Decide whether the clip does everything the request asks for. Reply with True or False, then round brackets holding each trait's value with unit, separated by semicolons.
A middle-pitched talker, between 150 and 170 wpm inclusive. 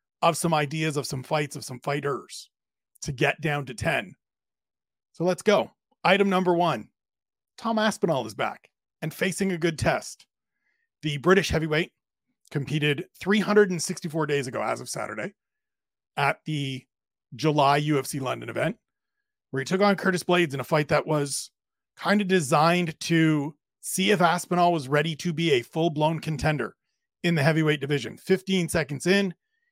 True (165 Hz; 155 wpm)